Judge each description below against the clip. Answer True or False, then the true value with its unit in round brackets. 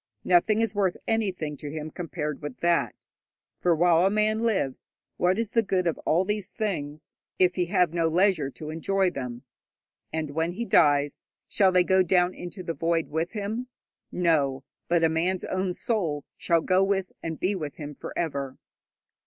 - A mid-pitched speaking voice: True (175 Hz)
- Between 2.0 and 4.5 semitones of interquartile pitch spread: True (3.5 semitones)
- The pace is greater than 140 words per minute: True (180 wpm)